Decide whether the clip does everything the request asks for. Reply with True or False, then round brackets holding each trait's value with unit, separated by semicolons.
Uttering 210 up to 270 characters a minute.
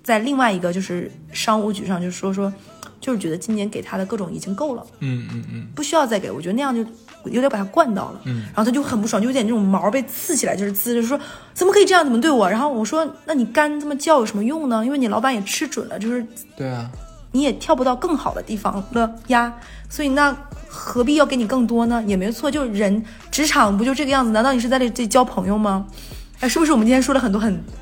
False (370 characters per minute)